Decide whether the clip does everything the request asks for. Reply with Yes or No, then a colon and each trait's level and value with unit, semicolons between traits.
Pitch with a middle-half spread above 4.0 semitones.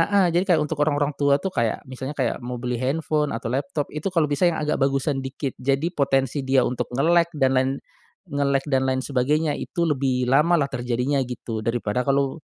No: average, 2.7 semitones